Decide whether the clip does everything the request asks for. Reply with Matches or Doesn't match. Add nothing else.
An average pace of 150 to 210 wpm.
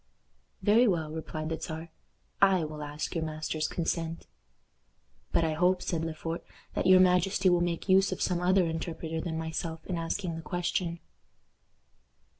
Matches